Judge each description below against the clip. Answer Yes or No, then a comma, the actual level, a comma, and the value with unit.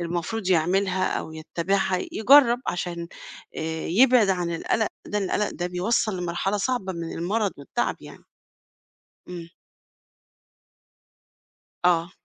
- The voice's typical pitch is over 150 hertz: Yes, medium, 185 Hz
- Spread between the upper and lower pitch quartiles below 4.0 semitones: Yes, average, 3.4 semitones